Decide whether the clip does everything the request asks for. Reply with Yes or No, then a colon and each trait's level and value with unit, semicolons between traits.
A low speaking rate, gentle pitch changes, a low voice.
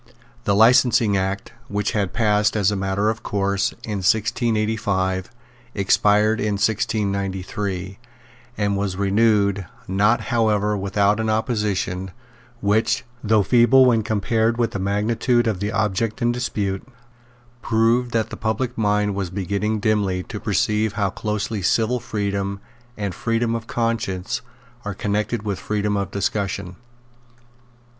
Yes: slow, 130 wpm; narrow, 2.1 semitones; low, 105 Hz